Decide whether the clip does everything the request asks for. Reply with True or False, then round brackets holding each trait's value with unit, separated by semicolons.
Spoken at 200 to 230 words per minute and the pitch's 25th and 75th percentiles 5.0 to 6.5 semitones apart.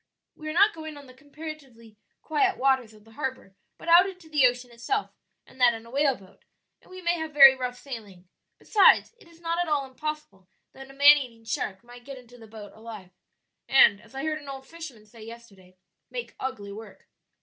True (205 wpm; 5.3 semitones)